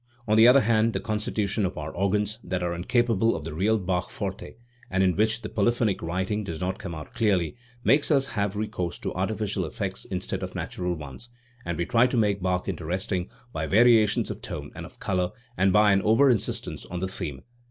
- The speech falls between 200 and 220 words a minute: Yes, fast, 205 wpm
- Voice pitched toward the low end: Yes, low, 100 Hz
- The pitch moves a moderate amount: Yes, average, 3.4 semitones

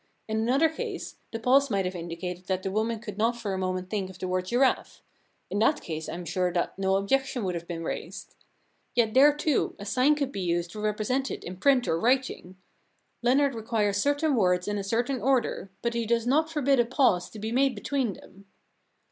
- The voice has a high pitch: Yes, high, 220 Hz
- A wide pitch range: Yes, wide, 5.8 semitones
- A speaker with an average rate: No, fast, 220 wpm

